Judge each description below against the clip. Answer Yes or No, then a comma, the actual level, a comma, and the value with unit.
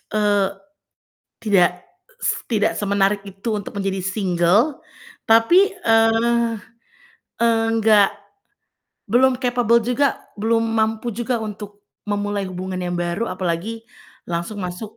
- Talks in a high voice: Yes, high, 215 Hz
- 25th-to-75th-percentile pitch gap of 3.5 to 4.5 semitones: No, average, 2.9 semitones